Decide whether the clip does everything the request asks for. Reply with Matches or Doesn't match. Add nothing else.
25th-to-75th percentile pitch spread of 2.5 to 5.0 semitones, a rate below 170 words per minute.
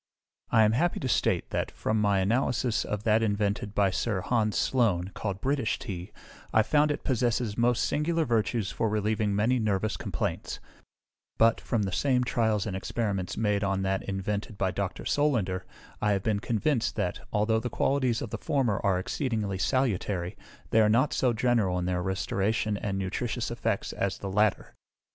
Doesn't match